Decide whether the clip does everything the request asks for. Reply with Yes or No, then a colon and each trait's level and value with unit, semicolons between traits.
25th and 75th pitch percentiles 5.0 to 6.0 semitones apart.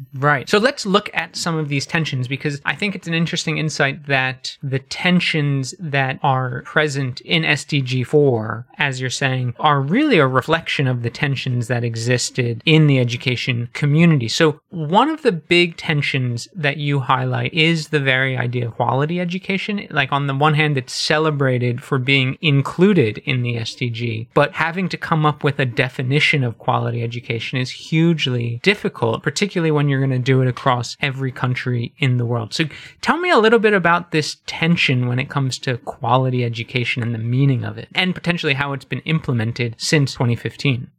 No: average, 4.1 semitones